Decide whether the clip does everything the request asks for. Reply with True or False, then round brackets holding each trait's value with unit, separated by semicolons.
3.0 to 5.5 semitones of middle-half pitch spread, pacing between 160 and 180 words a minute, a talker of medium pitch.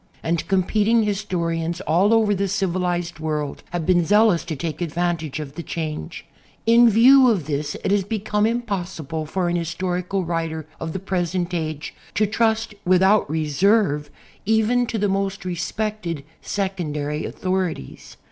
False (4.1 semitones; 145 wpm; 180 Hz)